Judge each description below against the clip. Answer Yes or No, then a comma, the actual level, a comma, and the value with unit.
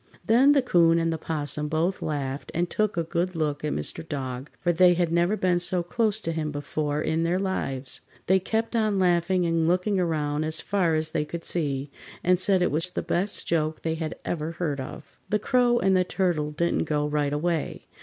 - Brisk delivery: Yes, fast, 210 wpm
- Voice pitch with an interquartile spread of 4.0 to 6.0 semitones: No, average, 3.3 semitones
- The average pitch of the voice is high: No, medium, 165 Hz